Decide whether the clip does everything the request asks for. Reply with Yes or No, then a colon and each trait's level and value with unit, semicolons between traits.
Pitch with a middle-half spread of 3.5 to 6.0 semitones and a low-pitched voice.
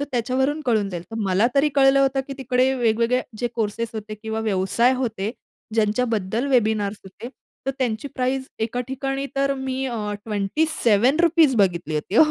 No: average, 3.9 semitones; high, 240 Hz